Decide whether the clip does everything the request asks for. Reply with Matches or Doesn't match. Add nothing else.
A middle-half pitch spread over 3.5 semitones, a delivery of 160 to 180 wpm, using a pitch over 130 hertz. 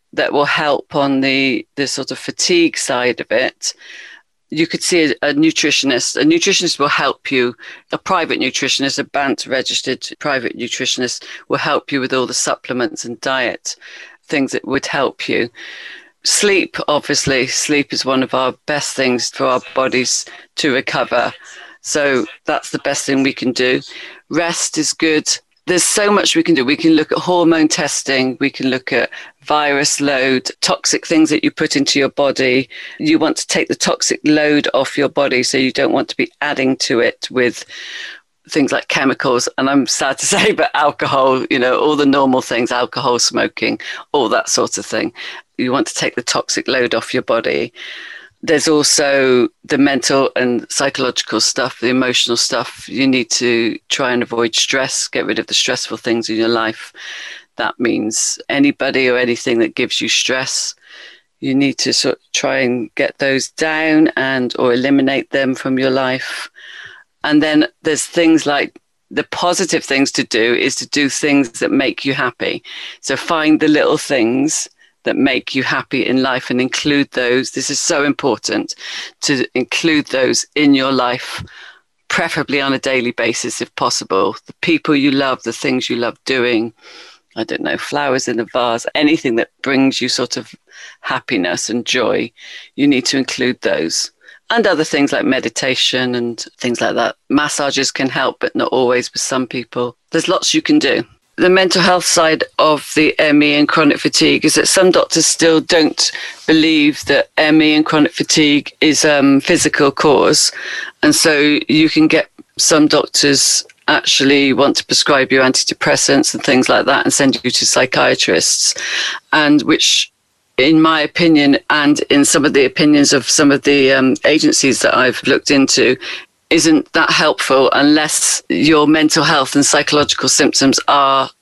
Doesn't match